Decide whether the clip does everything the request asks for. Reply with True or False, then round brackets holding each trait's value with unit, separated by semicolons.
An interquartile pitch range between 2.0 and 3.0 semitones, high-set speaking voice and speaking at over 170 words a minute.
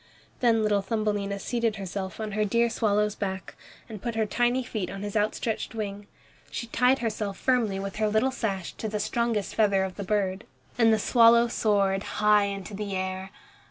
True (2.4 semitones; 210 Hz; 185 wpm)